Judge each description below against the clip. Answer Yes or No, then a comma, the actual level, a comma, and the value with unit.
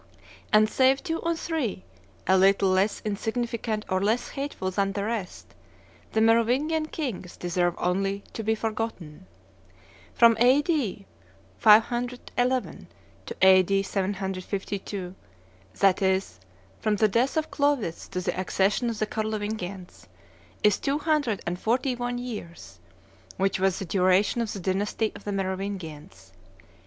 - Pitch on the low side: No, high, 205 Hz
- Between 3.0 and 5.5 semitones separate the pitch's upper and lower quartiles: Yes, average, 4.2 semitones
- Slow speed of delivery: Yes, slow, 130 wpm